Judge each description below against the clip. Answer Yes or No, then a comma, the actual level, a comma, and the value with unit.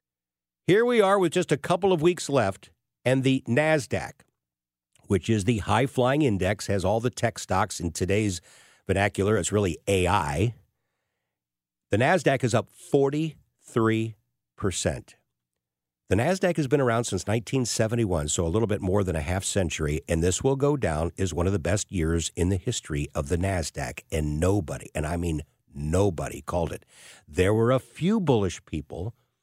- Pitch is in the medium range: No, low, 100 Hz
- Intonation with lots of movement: Yes, wide, 6.7 semitones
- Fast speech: No, average, 165 wpm